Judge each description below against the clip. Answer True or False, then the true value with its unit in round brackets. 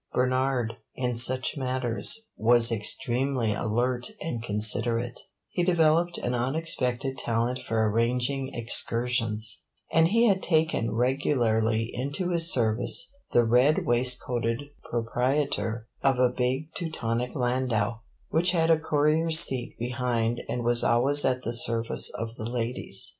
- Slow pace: True (125 wpm)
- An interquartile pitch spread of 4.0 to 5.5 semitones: False (3.3 semitones)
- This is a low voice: True (125 Hz)